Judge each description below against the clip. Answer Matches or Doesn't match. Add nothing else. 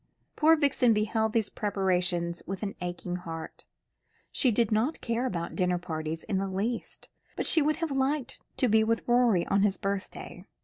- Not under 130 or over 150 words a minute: Doesn't match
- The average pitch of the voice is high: Matches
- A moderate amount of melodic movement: Matches